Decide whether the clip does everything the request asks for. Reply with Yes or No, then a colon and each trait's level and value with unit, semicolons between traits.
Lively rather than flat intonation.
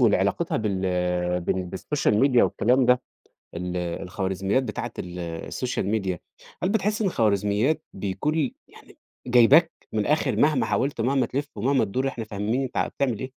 Yes: wide, 5.8 semitones